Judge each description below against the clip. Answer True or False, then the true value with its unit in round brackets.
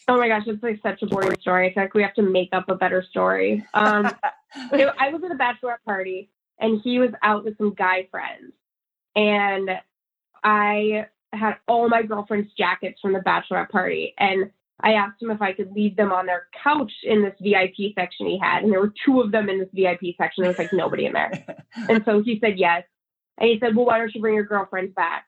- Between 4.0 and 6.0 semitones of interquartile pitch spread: False (3.0 semitones)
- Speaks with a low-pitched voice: False (210 Hz)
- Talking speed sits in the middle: False (225 wpm)